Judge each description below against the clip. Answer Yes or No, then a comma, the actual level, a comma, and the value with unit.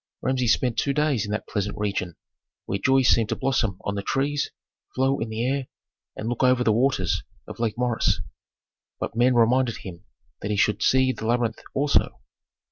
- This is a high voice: No, low, 120 Hz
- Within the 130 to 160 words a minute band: No, average, 185 wpm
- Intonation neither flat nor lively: Yes, average, 3.6 semitones